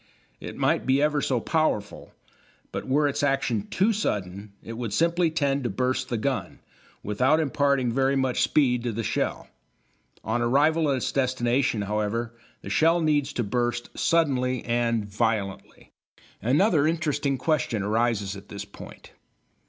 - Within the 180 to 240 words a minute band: No, average, 150 wpm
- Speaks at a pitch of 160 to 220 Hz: No, low, 130 Hz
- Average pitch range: Yes, average, 4.2 semitones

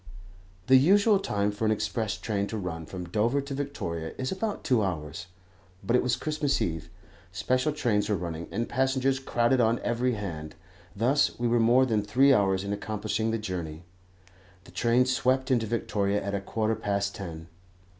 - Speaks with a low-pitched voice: Yes, low, 110 Hz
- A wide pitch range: No, average, 4.4 semitones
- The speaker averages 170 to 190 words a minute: Yes, average, 175 wpm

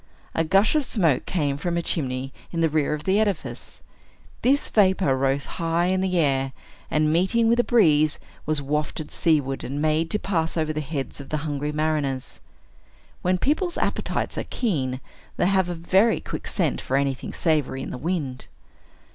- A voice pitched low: No, medium, 155 Hz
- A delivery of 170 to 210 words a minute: Yes, average, 180 wpm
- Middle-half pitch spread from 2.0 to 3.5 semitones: No, average, 4.8 semitones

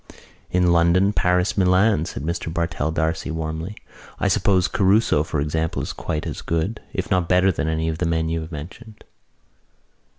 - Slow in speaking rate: No, average, 170 wpm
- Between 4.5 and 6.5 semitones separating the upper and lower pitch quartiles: No, narrow, 2.4 semitones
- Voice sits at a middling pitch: No, very low, 85 Hz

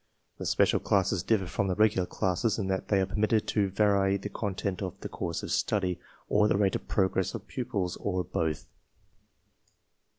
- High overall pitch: No, very low, 95 Hz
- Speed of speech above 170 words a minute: Yes, average, 185 wpm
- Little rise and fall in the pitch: Yes, narrow, 2.1 semitones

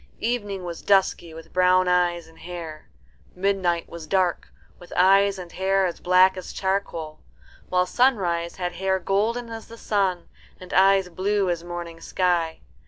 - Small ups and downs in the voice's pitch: Yes, narrow, 2.1 semitones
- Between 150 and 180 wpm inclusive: Yes, average, 155 wpm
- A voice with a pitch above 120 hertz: Yes, medium, 185 Hz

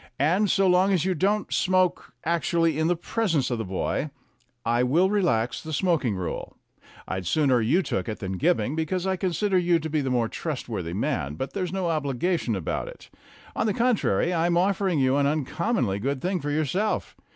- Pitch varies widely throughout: Yes, wide, 6.4 semitones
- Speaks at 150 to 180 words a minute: No, average, 195 wpm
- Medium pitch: Yes, medium, 160 Hz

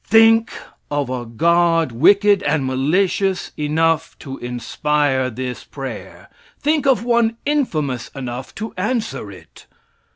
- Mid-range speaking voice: Yes, medium, 160 Hz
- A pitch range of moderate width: No, wide, 8.3 semitones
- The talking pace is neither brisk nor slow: No, slow, 120 wpm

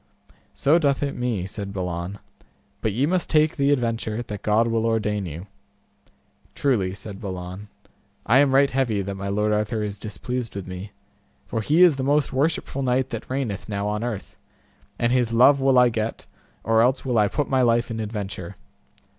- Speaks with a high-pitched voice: No, low, 115 Hz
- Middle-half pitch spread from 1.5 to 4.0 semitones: No, average, 4.4 semitones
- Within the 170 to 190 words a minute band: Yes, average, 185 wpm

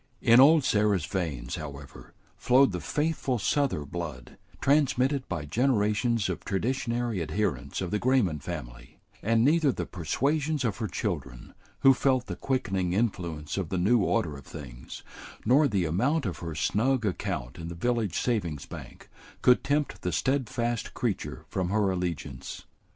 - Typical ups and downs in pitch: No, wide, 7.3 semitones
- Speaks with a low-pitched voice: Yes, low, 105 Hz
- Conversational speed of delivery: Yes, average, 150 wpm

